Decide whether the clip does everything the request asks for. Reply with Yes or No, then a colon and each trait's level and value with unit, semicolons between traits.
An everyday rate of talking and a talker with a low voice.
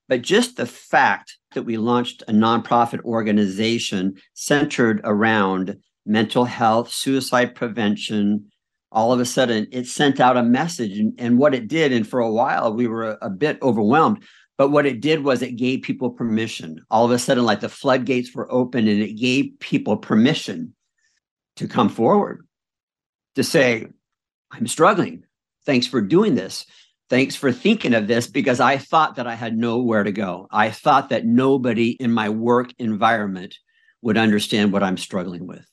Yes: average, 170 wpm; low, 120 Hz